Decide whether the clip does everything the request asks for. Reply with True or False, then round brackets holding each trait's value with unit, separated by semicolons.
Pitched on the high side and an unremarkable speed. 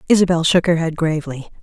False (165 Hz; 185 wpm)